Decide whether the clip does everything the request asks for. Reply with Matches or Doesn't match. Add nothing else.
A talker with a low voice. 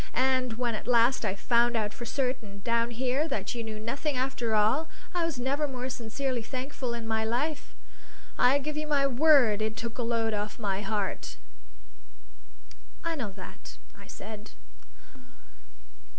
Doesn't match